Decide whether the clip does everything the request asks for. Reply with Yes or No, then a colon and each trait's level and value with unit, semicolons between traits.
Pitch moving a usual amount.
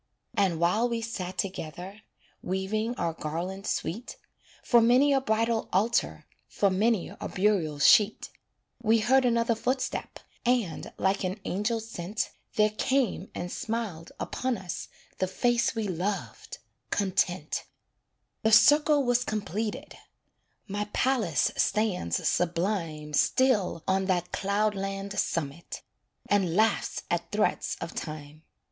Yes: average, 4.2 semitones